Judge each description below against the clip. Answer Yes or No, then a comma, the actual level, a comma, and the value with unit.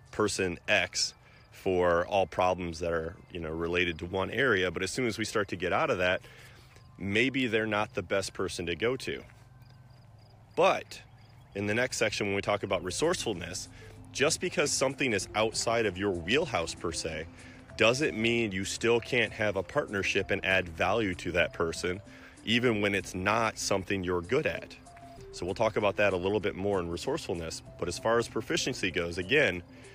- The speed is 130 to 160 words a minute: No, average, 195 wpm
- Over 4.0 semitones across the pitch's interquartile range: Yes, average, 4.6 semitones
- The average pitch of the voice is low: Yes, low, 105 Hz